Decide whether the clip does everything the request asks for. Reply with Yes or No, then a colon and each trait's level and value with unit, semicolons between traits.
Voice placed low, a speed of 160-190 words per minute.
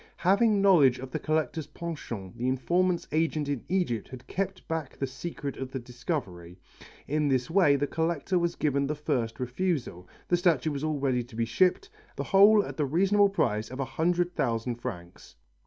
No: medium, 145 Hz; average, 185 wpm